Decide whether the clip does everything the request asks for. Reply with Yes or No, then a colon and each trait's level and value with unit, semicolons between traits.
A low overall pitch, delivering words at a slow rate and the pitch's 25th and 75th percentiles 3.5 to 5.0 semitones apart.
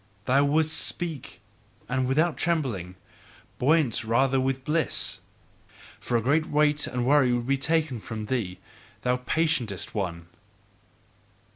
Yes: low, 130 Hz; slow, 125 wpm; average, 4.2 semitones